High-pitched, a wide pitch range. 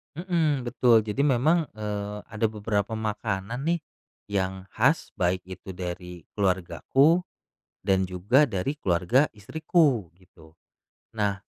No: low, 105 Hz; wide, 6.0 semitones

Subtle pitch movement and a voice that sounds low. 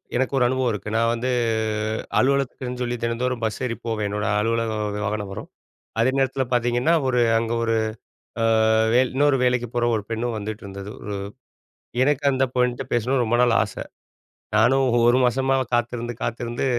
Yes: narrow, 2.2 semitones; low, 120 Hz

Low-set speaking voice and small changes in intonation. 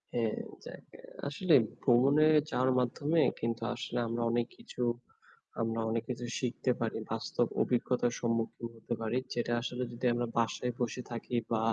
Yes: low, 120 Hz; narrow, 1.5 semitones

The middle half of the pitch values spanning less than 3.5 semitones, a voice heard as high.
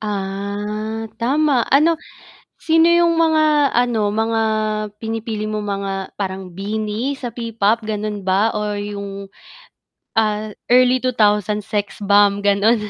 Yes: average, 3.0 semitones; high, 215 Hz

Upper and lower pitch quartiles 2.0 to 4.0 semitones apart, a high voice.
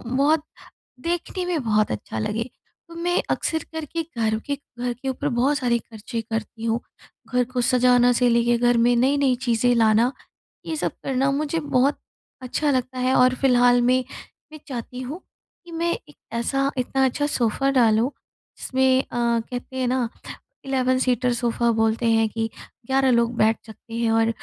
Yes: narrow, 2.6 semitones; very high, 250 Hz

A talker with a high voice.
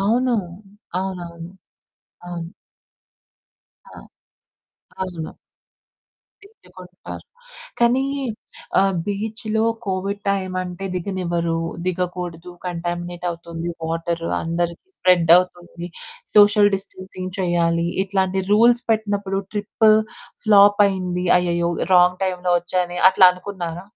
No: medium, 180 Hz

